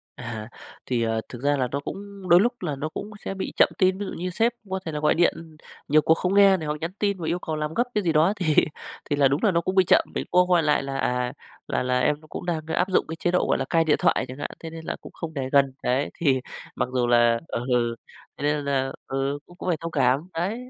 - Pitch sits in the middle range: Yes, medium, 155 Hz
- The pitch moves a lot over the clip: No, average, 4.7 semitones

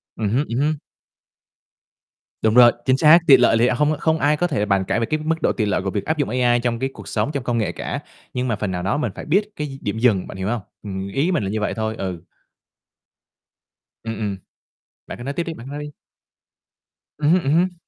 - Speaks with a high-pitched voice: No, low, 125 Hz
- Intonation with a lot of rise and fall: Yes, wide, 6.0 semitones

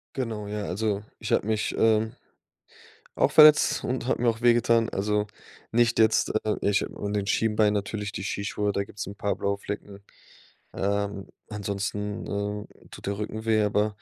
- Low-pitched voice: Yes, low, 105 Hz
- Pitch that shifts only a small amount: Yes, narrow, 1.5 semitones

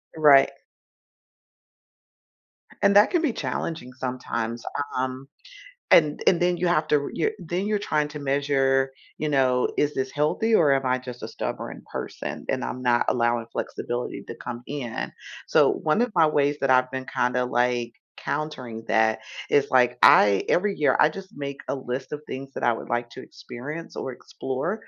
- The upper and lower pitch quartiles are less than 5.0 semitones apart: Yes, average, 3.6 semitones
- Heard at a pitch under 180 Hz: Yes, low, 135 Hz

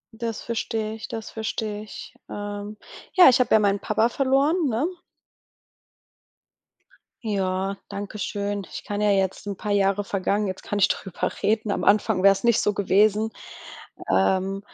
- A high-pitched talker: Yes, high, 205 Hz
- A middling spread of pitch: No, narrow, 1.9 semitones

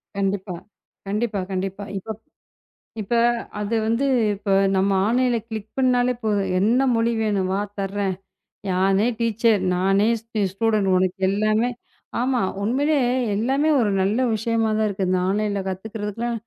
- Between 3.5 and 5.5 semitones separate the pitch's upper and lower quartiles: No, average, 3.0 semitones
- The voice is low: No, high, 210 Hz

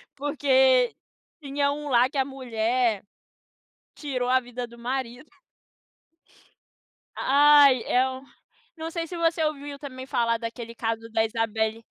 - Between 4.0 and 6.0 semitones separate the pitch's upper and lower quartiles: No, average, 3.4 semitones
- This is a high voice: Yes, very high, 260 Hz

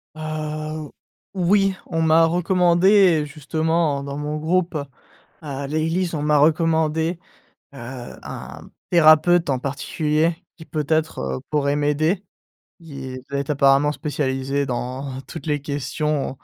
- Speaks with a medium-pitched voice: Yes, medium, 155 Hz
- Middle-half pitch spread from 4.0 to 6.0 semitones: No, narrow, 2.6 semitones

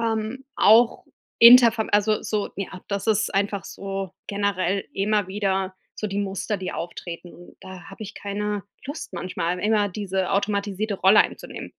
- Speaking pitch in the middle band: No, high, 200 Hz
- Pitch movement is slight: Yes, narrow, 1.9 semitones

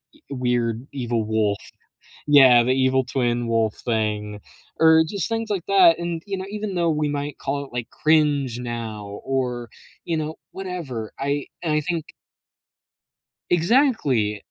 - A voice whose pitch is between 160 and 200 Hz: No, medium, 140 Hz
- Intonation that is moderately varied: No, wide, 5.8 semitones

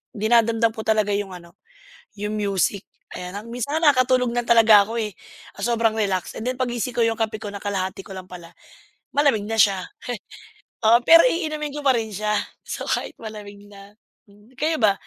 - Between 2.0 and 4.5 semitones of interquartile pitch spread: Yes, average, 3.0 semitones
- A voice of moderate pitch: No, high, 220 Hz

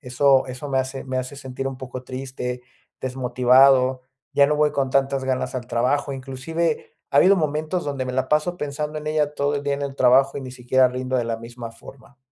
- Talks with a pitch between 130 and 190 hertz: Yes, low, 135 Hz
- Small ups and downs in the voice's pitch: Yes, narrow, 1.9 semitones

